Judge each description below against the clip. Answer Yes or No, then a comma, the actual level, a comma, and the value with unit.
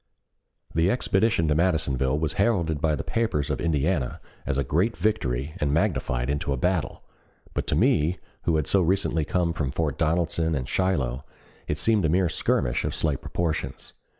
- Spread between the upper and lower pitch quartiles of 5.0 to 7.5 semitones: No, average, 4.0 semitones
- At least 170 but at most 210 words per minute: Yes, average, 175 wpm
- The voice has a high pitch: No, very low, 80 Hz